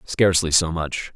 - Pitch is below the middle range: Yes, very low, 85 Hz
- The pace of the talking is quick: No, average, 155 wpm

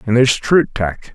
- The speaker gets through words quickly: Yes, fast, 210 wpm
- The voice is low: Yes, low, 120 Hz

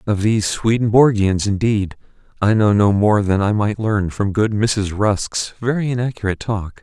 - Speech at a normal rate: Yes, average, 165 wpm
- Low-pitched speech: Yes, low, 105 Hz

